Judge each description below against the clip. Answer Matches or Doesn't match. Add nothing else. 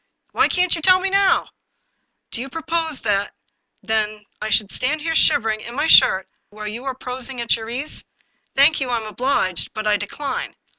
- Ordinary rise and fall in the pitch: Doesn't match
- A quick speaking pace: Matches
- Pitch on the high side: Matches